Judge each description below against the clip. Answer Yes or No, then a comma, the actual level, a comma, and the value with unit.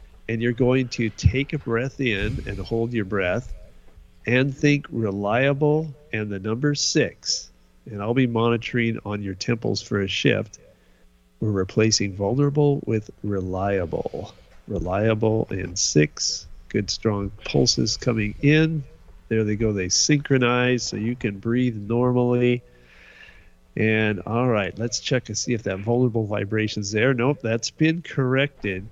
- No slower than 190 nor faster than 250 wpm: No, average, 140 wpm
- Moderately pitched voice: No, low, 110 Hz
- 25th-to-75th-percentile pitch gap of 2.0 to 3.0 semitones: No, average, 3.8 semitones